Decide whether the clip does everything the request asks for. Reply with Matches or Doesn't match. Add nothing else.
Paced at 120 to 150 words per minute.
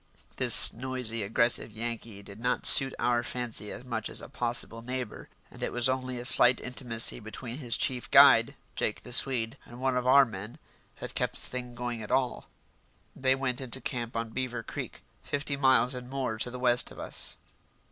Doesn't match